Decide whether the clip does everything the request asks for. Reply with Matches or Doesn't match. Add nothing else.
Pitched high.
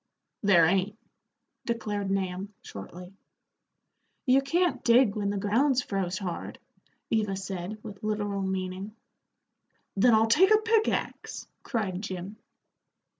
Matches